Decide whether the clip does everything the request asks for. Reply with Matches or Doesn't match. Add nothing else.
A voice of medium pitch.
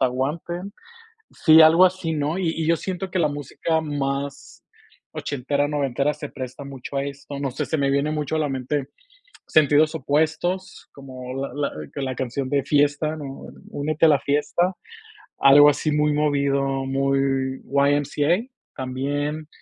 Matches